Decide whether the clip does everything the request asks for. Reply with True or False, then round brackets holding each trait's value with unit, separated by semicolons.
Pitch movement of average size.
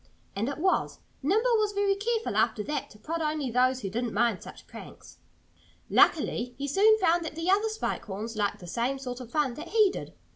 False (8.6 semitones)